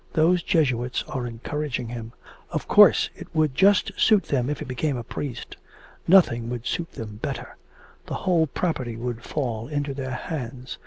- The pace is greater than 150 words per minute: Yes, average, 165 wpm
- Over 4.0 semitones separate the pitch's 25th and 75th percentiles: Yes, average, 4.6 semitones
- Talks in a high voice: No, low, 130 Hz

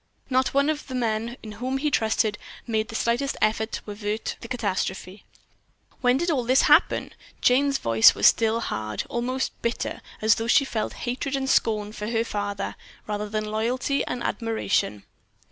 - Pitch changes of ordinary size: Yes, average, 3.2 semitones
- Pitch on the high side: Yes, high, 230 Hz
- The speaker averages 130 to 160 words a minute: No, average, 180 wpm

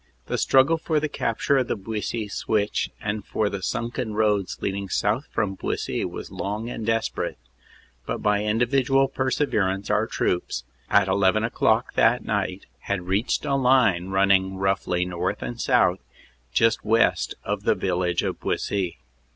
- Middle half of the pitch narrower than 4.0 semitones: Yes, average, 3.6 semitones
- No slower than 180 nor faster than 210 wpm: No, average, 160 wpm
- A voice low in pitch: Yes, low, 105 Hz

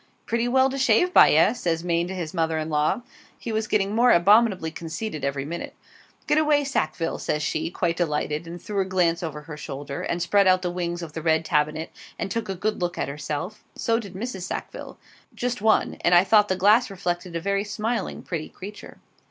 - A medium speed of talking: No, fast, 210 wpm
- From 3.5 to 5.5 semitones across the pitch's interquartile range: Yes, average, 4.7 semitones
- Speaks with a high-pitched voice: No, medium, 180 Hz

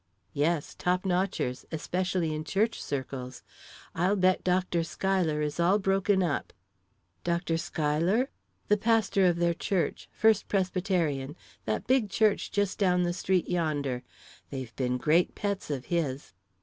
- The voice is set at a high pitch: No, medium, 175 Hz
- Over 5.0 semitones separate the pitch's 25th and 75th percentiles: No, average, 4.1 semitones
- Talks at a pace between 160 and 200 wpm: No, slow, 135 wpm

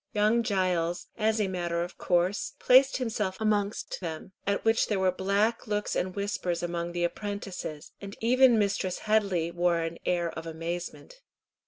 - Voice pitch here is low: No, high, 190 Hz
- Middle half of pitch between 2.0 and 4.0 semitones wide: Yes, average, 3.6 semitones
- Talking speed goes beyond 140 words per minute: Yes, average, 160 wpm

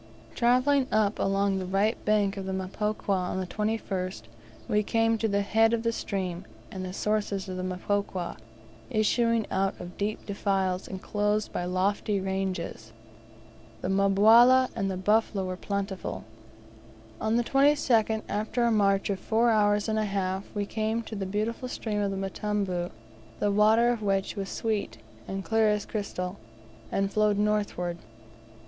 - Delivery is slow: No, average, 155 wpm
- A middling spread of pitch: No, narrow, 2.2 semitones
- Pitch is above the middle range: Yes, high, 205 Hz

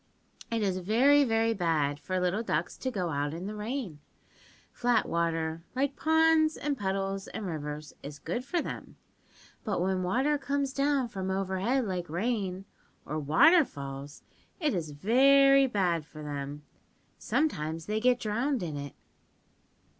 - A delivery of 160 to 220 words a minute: No, average, 150 wpm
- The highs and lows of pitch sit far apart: Yes, wide, 8.1 semitones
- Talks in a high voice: Yes, high, 195 Hz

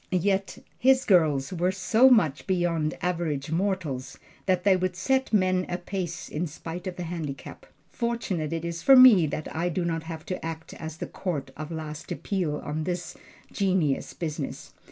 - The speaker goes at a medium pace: Yes, average, 175 wpm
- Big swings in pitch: No, average, 3.1 semitones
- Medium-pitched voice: Yes, medium, 175 Hz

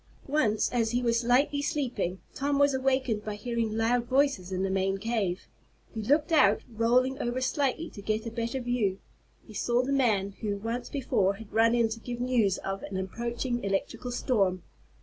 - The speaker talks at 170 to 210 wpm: Yes, average, 185 wpm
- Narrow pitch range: No, average, 3.7 semitones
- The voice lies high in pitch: Yes, high, 235 Hz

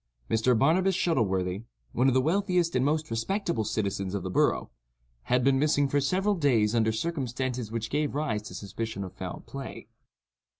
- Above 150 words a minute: Yes, average, 160 wpm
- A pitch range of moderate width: No, wide, 6.1 semitones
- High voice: No, low, 125 Hz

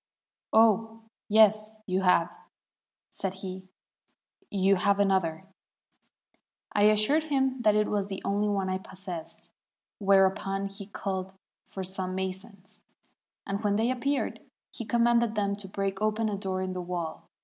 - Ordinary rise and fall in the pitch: No, narrow, 2.1 semitones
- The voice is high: Yes, high, 200 Hz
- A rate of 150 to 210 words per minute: No, average, 140 wpm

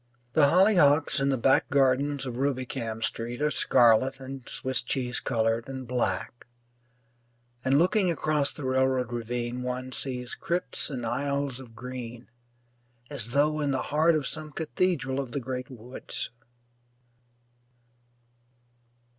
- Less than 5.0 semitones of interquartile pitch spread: Yes, average, 2.7 semitones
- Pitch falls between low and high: No, low, 130 Hz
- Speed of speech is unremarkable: No, slow, 130 wpm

